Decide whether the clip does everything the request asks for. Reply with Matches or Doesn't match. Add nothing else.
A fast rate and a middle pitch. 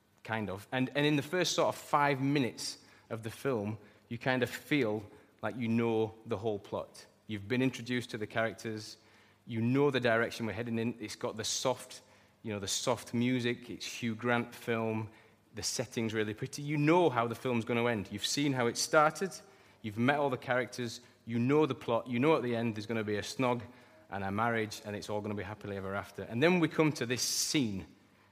Doesn't match